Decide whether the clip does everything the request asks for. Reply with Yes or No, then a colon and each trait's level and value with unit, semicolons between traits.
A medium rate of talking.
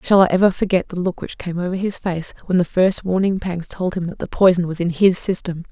No: fast, 260 wpm